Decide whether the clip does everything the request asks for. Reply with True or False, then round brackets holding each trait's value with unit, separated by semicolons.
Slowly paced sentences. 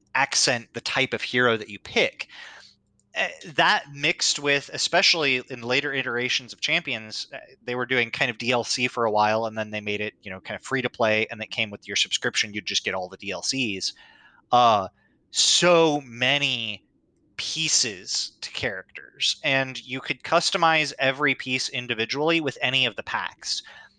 False (170 wpm)